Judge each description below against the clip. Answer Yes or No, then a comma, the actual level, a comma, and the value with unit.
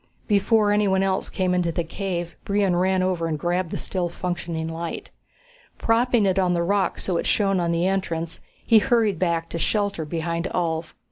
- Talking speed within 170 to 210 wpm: Yes, average, 185 wpm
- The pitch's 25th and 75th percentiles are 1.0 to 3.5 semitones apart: Yes, average, 2.7 semitones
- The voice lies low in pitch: No, medium, 180 Hz